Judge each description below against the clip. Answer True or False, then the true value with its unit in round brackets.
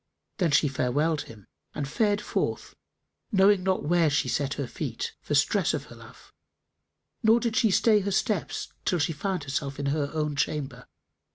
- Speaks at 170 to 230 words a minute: True (175 wpm)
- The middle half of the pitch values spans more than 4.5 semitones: True (5.6 semitones)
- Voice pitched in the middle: True (155 Hz)